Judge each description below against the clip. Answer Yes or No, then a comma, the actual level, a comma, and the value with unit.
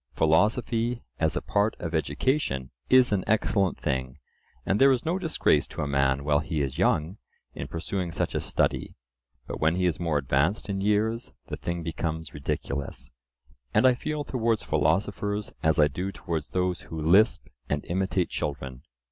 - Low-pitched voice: Yes, very low, 85 Hz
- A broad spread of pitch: Yes, wide, 6.1 semitones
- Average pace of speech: Yes, average, 170 wpm